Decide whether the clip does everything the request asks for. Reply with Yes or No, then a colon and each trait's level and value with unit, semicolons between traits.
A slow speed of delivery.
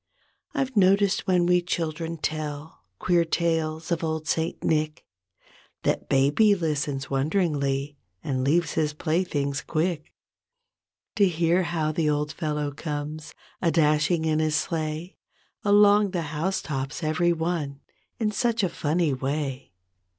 Yes: slow, 130 wpm